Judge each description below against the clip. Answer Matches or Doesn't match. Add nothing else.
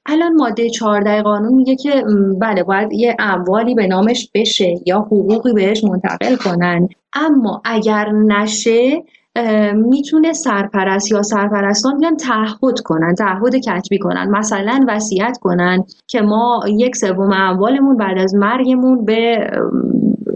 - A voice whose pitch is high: Matches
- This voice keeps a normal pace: Matches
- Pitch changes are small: Doesn't match